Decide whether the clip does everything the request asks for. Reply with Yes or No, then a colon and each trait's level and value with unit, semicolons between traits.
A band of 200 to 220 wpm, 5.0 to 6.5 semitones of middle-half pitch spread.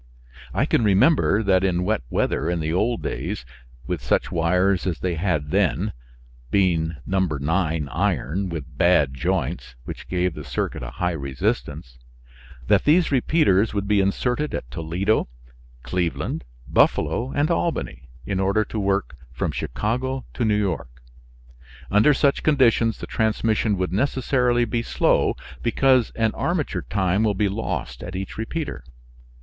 No: average, 145 wpm; average, 5.3 semitones